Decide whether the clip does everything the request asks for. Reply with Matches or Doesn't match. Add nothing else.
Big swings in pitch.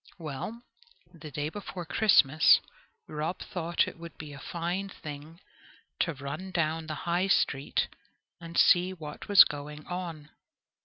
Doesn't match